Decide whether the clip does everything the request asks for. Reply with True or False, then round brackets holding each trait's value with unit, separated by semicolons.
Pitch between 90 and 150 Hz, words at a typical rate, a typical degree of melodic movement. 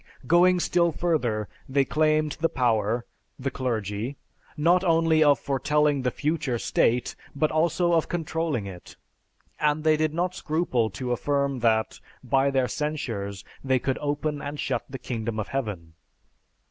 True (140 Hz; 145 wpm; 4.6 semitones)